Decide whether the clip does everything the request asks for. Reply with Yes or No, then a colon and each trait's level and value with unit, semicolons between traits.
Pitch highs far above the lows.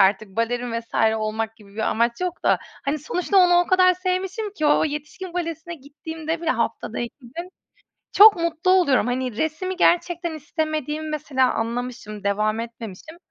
Yes: wide, 6.9 semitones